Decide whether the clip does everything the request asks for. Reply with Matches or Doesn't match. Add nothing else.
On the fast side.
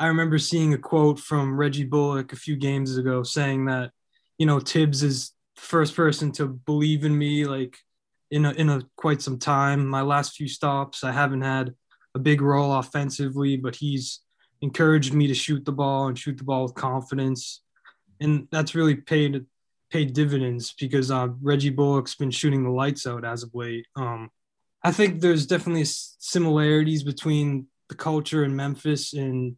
Doesn't match